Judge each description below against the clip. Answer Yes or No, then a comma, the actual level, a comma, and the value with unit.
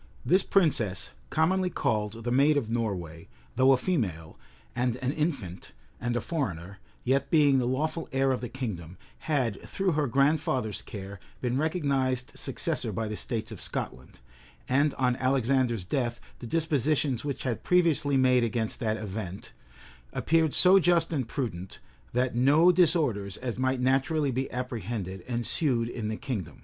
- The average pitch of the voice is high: No, low, 130 Hz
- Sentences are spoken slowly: No, average, 155 wpm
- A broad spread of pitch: No, average, 4.7 semitones